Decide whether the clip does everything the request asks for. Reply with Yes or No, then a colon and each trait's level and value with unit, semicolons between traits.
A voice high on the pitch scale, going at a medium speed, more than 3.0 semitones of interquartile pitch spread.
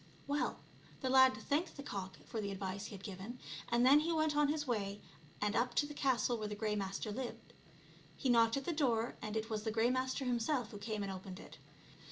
No: high, 230 Hz; fast, 230 wpm; average, 4.2 semitones